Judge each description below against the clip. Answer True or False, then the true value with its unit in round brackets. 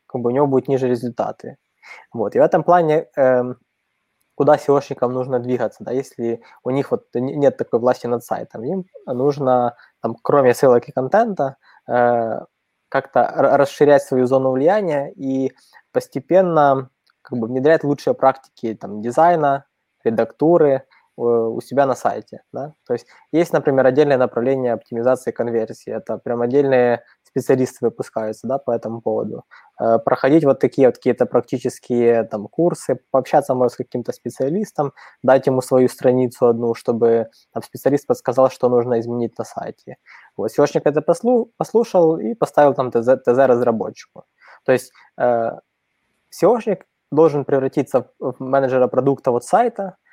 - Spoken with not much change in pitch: False (3.0 semitones)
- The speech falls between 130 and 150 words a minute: True (140 wpm)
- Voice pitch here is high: False (130 Hz)